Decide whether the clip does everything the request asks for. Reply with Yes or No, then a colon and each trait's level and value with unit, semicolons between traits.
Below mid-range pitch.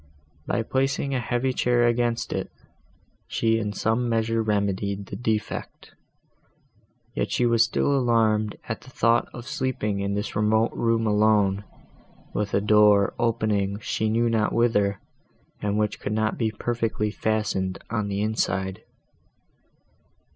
Yes: low, 110 Hz